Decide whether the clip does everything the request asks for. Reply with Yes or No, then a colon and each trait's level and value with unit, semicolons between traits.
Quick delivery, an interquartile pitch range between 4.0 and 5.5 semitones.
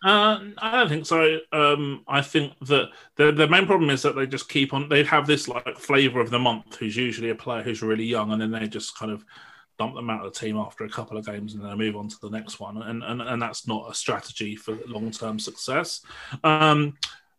Yes: fast, 250 wpm; average, 5.1 semitones